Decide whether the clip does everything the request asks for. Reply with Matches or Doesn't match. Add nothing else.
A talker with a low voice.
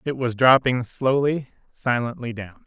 Matches